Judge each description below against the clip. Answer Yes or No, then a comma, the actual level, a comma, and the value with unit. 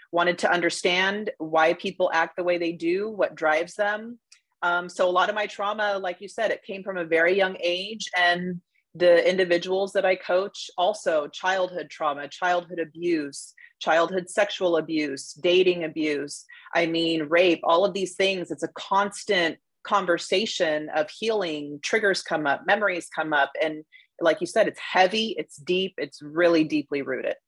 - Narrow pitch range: No, average, 3.1 semitones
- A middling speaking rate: Yes, average, 170 wpm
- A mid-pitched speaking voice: Yes, medium, 175 Hz